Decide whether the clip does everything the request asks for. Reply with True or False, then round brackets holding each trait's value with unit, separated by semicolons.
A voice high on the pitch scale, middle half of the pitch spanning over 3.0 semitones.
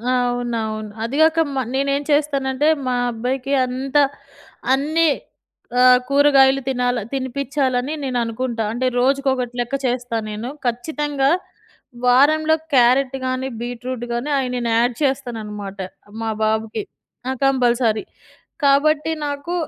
False (255 Hz; 2.5 semitones)